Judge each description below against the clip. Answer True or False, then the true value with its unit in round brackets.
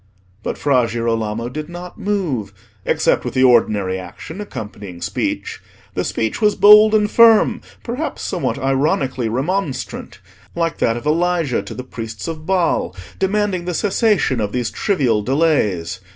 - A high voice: False (140 Hz)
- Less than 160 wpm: True (145 wpm)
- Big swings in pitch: True (8.6 semitones)